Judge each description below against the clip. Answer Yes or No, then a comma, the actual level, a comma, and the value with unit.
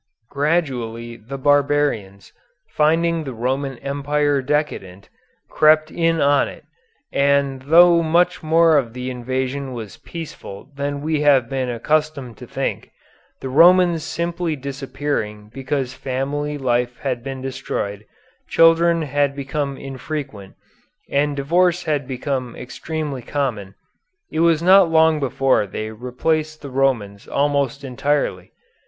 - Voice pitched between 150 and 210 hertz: No, medium, 140 Hz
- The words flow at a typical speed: No, slow, 125 wpm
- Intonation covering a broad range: No, average, 3.3 semitones